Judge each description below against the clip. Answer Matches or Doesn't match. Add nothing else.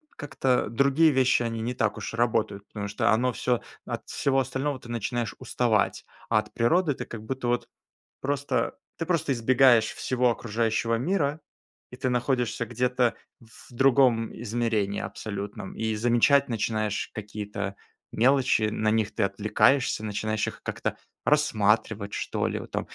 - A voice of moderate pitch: Doesn't match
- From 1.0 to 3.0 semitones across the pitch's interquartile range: Doesn't match